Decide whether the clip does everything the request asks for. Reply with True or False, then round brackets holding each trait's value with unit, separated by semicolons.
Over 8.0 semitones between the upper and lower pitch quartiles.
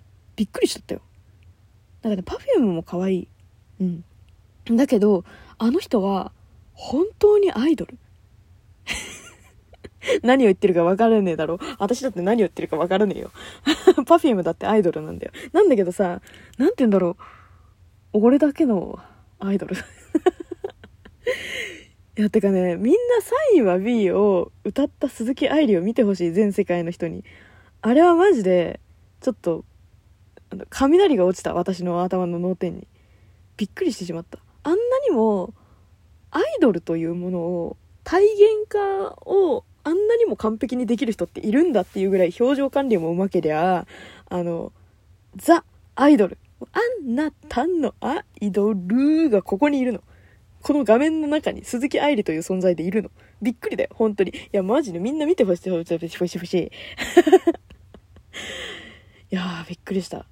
True (8.9 semitones)